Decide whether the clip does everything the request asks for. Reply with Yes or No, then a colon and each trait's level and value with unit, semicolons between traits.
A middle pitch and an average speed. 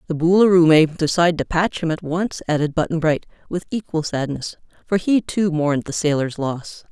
Yes: medium, 165 Hz; average, 190 wpm